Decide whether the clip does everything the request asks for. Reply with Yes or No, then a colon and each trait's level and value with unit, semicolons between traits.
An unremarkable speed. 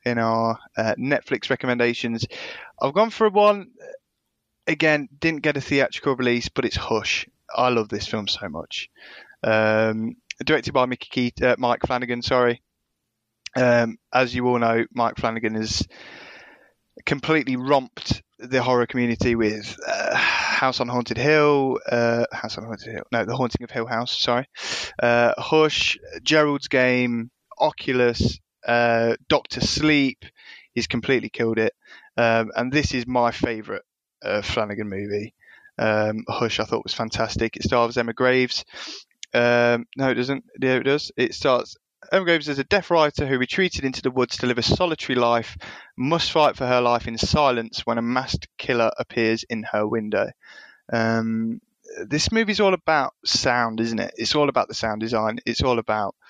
Yes: average, 160 wpm